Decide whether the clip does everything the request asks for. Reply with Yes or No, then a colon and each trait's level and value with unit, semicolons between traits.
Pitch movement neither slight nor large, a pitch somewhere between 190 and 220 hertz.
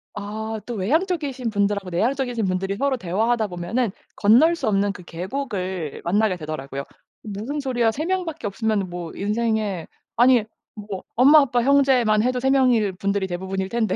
Yes: average, 4.9 semitones; high, 215 Hz